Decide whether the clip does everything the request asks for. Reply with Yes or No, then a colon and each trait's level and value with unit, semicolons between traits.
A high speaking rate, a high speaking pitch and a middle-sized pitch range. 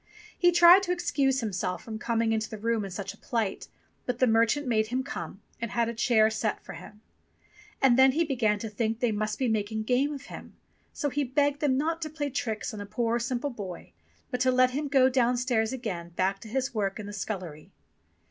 Yes: fast, 225 wpm; high, 235 Hz; average, 3.7 semitones